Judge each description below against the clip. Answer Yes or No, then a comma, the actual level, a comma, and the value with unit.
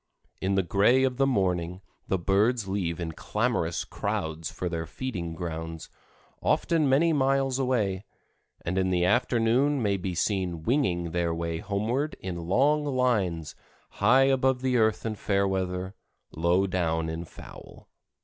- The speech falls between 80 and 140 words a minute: No, average, 150 wpm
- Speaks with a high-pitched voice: No, very low, 95 Hz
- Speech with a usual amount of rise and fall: No, wide, 6.6 semitones